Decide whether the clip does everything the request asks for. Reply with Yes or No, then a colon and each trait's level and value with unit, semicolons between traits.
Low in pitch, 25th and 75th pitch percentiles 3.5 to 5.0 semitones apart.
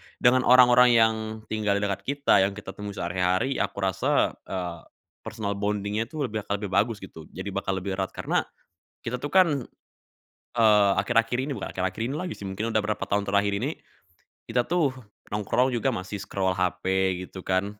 Yes: low, 105 Hz; average, 4.1 semitones